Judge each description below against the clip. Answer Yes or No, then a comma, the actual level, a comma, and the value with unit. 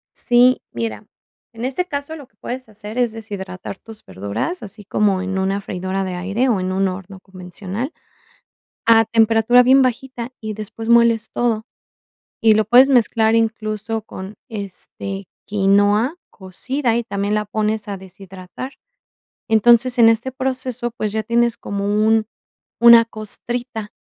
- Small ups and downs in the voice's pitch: No, average, 3.3 semitones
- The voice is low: No, high, 220 Hz